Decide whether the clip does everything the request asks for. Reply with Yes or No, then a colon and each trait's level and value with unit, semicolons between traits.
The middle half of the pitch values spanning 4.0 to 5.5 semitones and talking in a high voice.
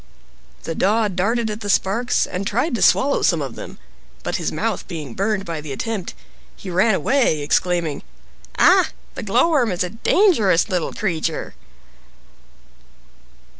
Yes: average, 5.0 semitones; high, 195 Hz